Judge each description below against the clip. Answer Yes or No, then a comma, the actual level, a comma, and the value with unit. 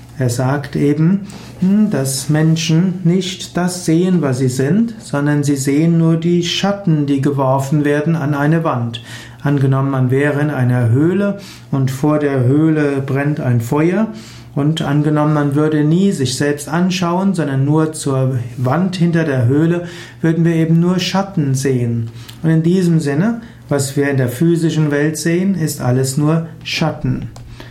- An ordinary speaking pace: Yes, average, 155 wpm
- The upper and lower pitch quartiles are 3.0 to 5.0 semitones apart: Yes, average, 3.8 semitones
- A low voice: No, medium, 150 Hz